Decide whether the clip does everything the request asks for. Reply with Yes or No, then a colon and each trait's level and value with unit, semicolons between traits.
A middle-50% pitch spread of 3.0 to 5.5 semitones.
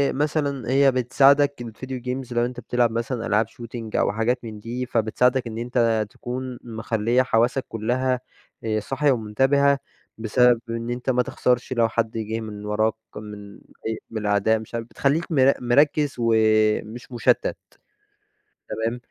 No: narrow, 2.5 semitones